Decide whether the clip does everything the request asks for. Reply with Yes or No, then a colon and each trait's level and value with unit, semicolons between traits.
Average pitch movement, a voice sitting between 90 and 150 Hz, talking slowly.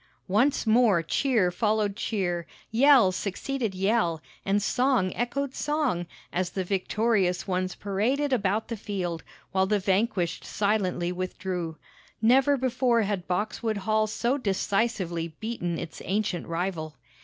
No: average, 4.2 semitones; high, 205 Hz; slow, 125 wpm